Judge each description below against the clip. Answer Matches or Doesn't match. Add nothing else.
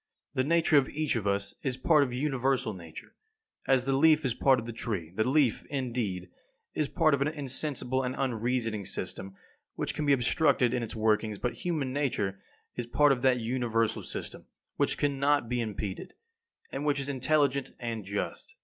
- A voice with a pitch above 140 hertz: Doesn't match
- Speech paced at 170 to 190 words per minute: Matches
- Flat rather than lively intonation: Doesn't match